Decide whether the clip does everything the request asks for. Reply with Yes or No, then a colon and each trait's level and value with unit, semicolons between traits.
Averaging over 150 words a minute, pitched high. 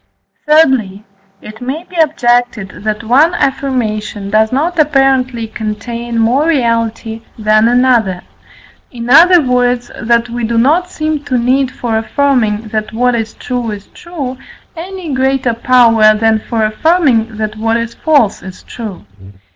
No: average, 140 wpm; high, 240 Hz